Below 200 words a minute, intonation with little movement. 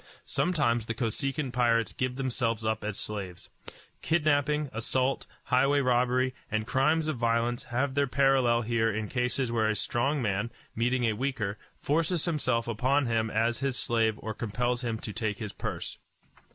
No: average, 160 wpm; average, 3.2 semitones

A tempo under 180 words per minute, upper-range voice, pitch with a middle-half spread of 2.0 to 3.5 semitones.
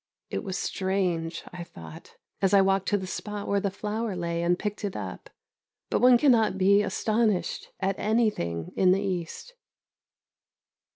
Yes: average, 160 wpm; high, 195 Hz; narrow, 2.5 semitones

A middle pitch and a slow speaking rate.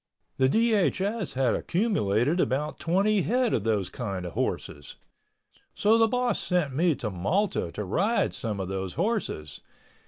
No: medium, 155 Hz; average, 150 wpm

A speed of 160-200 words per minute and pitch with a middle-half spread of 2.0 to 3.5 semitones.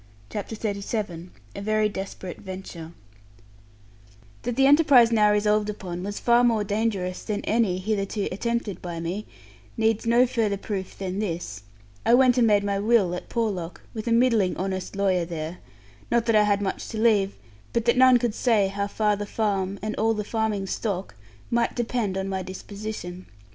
Yes: average, 175 wpm; average, 3.1 semitones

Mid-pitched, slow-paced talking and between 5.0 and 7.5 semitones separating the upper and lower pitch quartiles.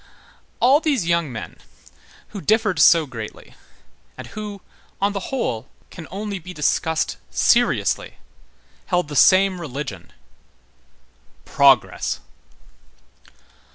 Yes: medium, 180 Hz; slow, 100 wpm; wide, 5.6 semitones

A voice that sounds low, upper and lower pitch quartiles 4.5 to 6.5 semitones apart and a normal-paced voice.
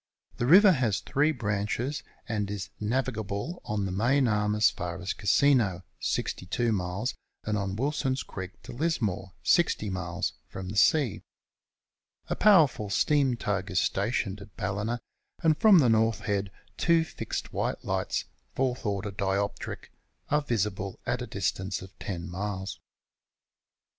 Yes: low, 105 Hz; average, 5.1 semitones; average, 145 wpm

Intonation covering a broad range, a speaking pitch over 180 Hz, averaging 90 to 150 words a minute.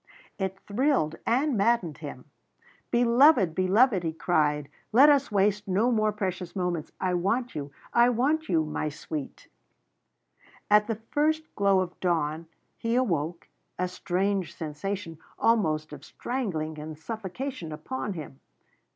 Yes: wide, 6.6 semitones; high, 190 Hz; slow, 135 wpm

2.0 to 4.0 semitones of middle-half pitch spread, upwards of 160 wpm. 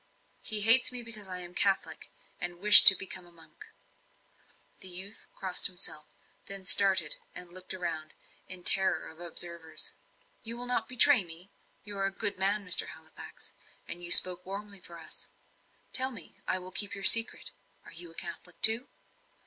Yes: average, 2.9 semitones; average, 175 wpm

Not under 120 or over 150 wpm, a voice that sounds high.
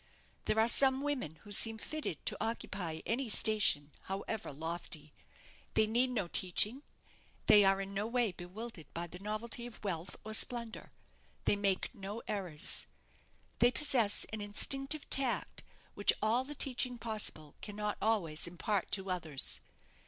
Yes: average, 145 wpm; high, 210 Hz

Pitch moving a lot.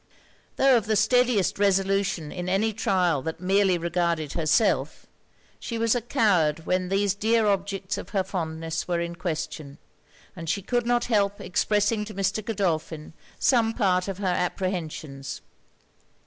No: average, 3.7 semitones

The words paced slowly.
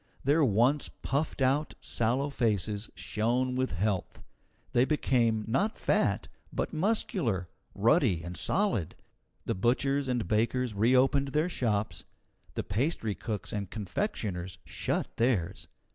Yes: slow, 120 wpm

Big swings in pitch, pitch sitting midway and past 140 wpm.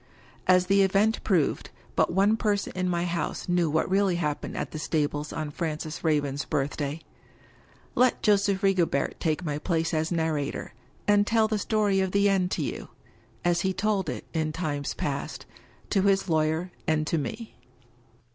No: average, 4.1 semitones; medium, 175 Hz; average, 170 wpm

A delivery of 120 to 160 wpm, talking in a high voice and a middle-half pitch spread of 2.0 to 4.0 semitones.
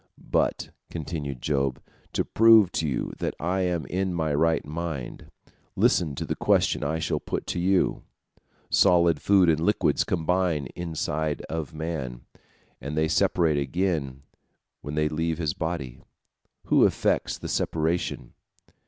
No: average, 140 wpm; very low, 80 Hz; average, 3.0 semitones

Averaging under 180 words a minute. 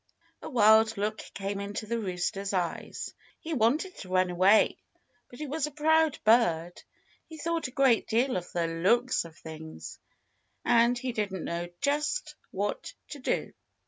Yes: average, 160 wpm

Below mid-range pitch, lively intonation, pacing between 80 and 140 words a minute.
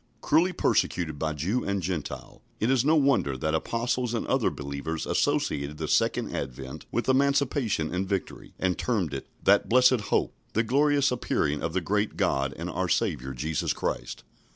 No: very low, 95 Hz; wide, 8.8 semitones; average, 170 wpm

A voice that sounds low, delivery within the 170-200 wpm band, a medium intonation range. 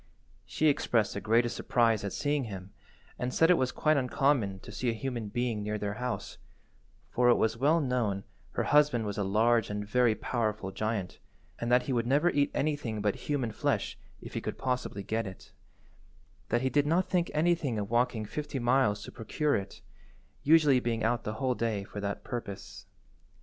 Yes: low, 120 Hz; average, 190 wpm; average, 4.3 semitones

